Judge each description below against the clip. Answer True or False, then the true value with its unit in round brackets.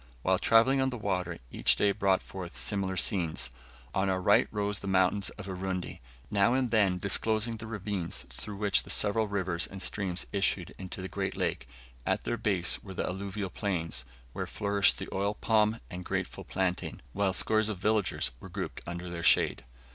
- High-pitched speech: False (100 Hz)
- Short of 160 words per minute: False (185 wpm)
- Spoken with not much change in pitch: True (2.3 semitones)